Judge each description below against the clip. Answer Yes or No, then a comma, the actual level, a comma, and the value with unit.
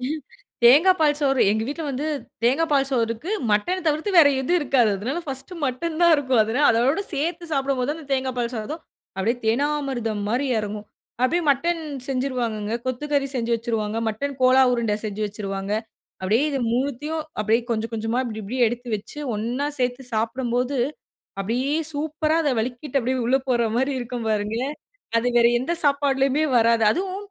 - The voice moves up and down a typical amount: Yes, average, 4.1 semitones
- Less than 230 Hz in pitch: No, very high, 255 Hz